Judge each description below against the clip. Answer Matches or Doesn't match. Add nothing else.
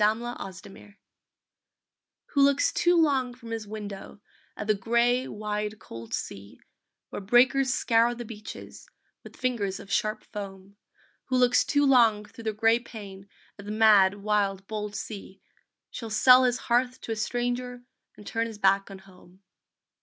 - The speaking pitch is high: Matches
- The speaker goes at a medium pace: Matches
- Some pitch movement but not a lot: Matches